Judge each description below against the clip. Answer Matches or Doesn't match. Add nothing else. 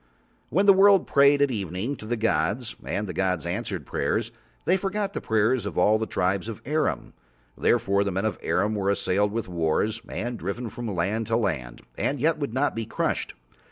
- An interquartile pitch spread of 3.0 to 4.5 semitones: Doesn't match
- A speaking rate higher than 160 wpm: Matches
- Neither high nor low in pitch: Doesn't match